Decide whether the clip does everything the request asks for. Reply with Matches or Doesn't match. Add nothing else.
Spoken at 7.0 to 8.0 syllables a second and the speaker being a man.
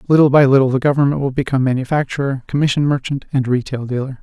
Matches